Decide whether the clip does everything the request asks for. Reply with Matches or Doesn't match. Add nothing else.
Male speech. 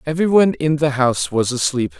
Matches